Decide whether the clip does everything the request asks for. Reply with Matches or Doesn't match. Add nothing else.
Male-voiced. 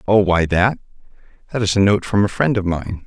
Matches